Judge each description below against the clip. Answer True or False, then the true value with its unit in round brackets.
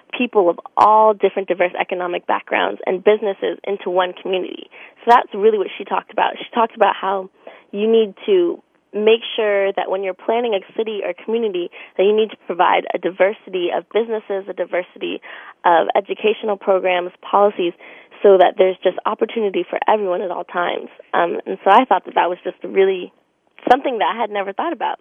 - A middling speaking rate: True (195 wpm)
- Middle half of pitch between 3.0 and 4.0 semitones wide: True (3.4 semitones)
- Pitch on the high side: True (205 Hz)